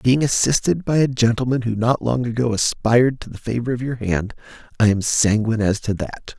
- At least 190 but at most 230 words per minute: Yes, fast, 205 wpm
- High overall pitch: No, low, 120 Hz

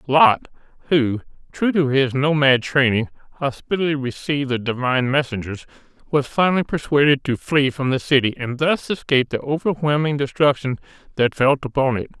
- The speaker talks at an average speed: Yes, average, 150 wpm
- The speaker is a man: Yes, male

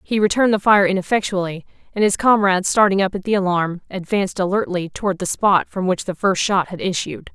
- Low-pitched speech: No, high, 190 Hz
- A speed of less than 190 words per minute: No, fast, 205 wpm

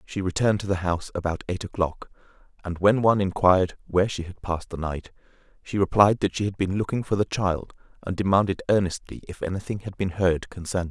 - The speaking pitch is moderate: No, very low, 95 Hz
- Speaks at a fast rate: Yes, fast, 210 wpm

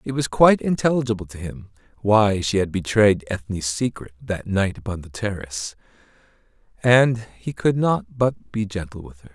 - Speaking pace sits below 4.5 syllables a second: No, 4.9 syllables/s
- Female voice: No, male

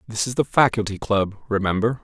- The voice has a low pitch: Yes, low, 110 Hz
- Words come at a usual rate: Yes, average, 175 wpm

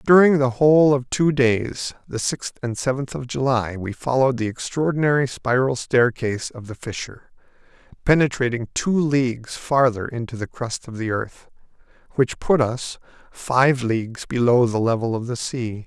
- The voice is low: Yes, low, 125 Hz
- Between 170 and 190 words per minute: No, average, 160 wpm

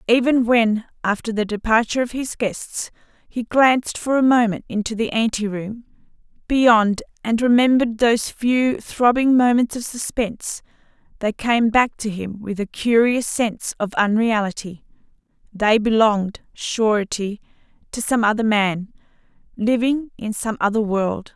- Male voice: No, female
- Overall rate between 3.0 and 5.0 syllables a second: Yes, 4.5 syllables/s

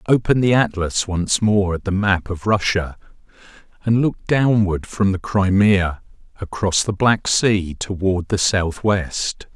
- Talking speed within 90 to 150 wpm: Yes, average, 145 wpm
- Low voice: Yes, low, 100 Hz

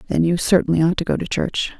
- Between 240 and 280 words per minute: Yes, fast, 265 wpm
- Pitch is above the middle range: No, medium, 170 Hz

